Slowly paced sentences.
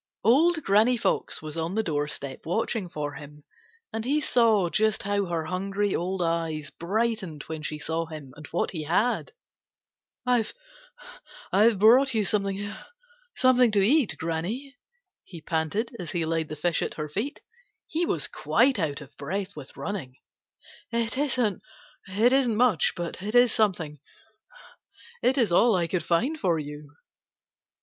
No: average, 145 wpm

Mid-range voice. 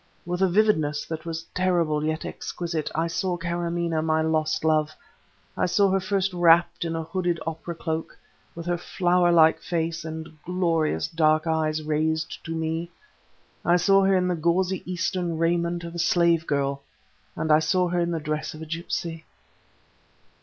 Yes: medium, 165 Hz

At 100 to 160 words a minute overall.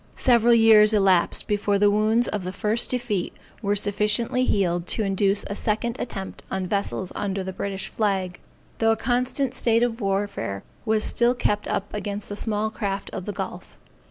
No: average, 175 wpm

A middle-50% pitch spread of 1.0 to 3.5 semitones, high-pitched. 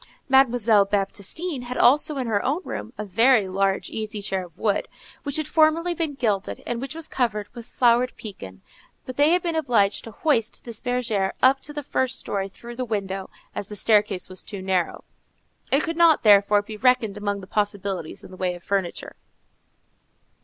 No: average, 4.9 semitones; high, 220 Hz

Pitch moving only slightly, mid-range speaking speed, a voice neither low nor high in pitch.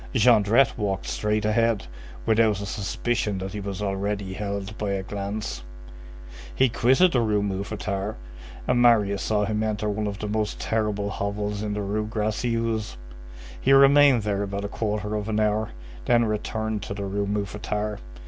No: narrow, 1.5 semitones; average, 165 wpm; low, 105 Hz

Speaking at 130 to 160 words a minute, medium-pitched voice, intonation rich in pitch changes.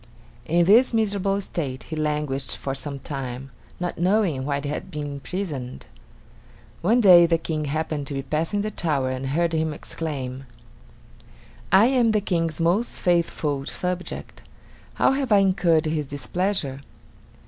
No: average, 150 wpm; medium, 160 Hz; average, 5.0 semitones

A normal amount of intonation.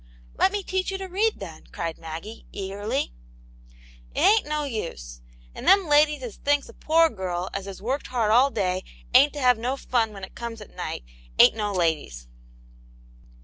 No: wide, 8.2 semitones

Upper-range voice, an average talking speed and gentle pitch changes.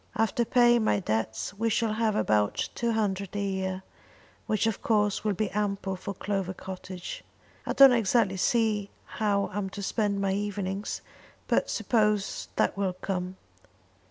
Yes: high, 200 Hz; average, 155 wpm; narrow, 2.2 semitones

